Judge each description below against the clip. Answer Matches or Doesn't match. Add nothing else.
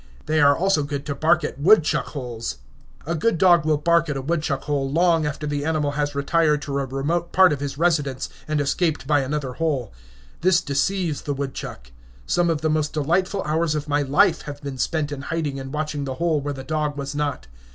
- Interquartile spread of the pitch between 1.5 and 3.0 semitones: Matches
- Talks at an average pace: Doesn't match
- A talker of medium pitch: Matches